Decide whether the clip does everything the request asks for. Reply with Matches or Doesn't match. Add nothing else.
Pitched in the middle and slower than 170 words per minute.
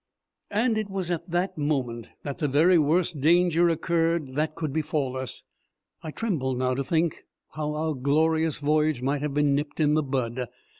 Doesn't match